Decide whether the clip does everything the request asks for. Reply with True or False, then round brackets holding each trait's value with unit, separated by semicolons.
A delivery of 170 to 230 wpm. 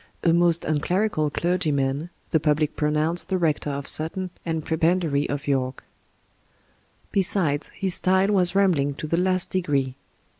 False (145 wpm)